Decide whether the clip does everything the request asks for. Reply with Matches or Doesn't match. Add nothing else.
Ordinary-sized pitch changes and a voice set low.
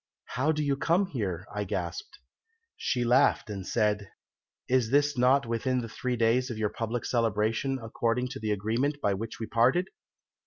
Matches